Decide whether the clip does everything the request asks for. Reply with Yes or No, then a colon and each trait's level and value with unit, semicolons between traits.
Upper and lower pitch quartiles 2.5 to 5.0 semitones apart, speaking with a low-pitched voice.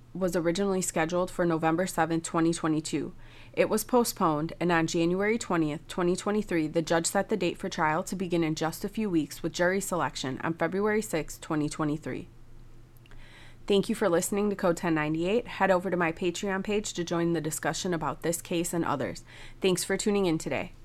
No: average, 3.2 semitones; medium, 170 Hz